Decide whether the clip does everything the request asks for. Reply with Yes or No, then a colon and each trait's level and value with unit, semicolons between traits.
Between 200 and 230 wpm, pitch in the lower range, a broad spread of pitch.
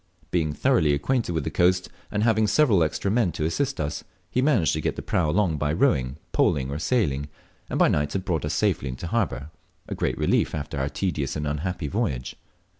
Yes: fast, 205 wpm; very low, 80 Hz; wide, 6.1 semitones